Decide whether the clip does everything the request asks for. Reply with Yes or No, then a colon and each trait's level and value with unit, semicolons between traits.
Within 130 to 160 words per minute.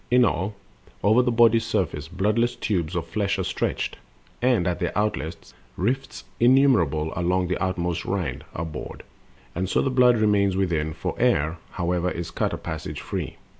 No: average, 170 wpm